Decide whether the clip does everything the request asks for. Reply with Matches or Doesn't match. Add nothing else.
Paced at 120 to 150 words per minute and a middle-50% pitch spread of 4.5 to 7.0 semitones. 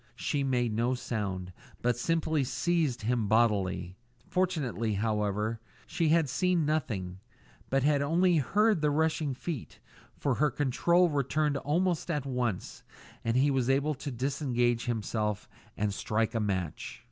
Matches